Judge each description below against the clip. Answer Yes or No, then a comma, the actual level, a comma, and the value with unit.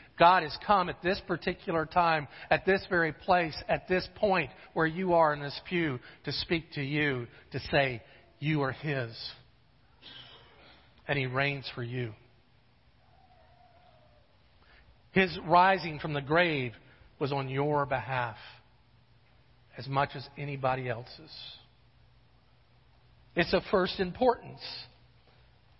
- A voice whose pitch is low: No, medium, 145 Hz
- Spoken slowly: Yes, slow, 120 wpm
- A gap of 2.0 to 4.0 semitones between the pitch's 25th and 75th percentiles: No, wide, 5.6 semitones